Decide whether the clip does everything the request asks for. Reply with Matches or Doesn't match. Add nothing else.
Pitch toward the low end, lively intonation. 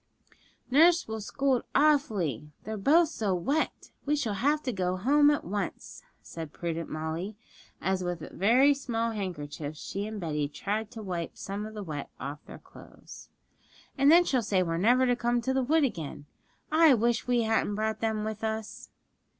Doesn't match